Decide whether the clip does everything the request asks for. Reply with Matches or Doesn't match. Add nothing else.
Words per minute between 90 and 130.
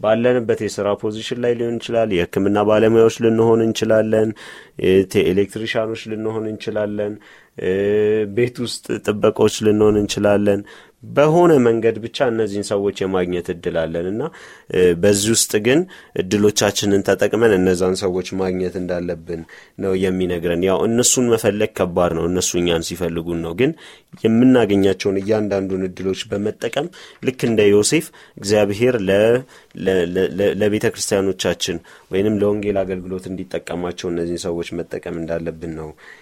Matches